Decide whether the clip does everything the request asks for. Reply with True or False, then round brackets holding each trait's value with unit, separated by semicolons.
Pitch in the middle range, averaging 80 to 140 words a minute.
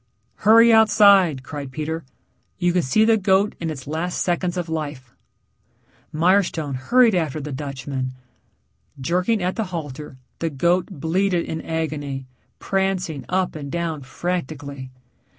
True (165 Hz; 135 wpm)